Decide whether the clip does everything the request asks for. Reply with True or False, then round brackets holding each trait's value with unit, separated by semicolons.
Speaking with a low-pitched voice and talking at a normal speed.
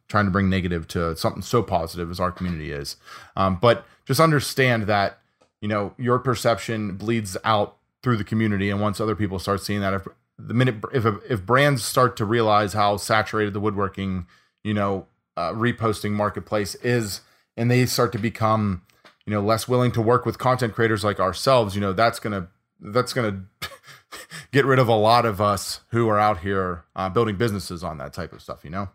True (105 Hz; 195 wpm)